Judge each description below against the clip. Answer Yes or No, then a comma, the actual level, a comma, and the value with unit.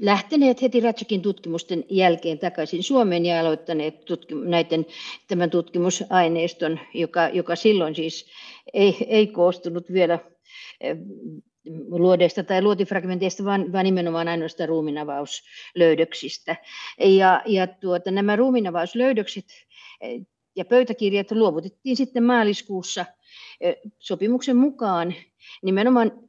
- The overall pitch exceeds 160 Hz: Yes, medium, 185 Hz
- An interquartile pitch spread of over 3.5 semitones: Yes, average, 3.9 semitones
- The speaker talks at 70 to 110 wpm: Yes, slow, 95 wpm